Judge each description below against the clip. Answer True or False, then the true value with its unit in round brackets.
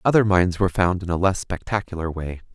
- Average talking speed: False (210 wpm)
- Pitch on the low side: True (90 Hz)